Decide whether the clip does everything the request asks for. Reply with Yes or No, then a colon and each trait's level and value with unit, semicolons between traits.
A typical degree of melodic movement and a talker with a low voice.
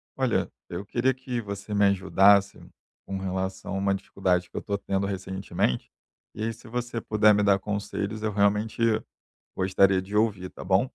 No: narrow, 1.8 semitones; low, 100 Hz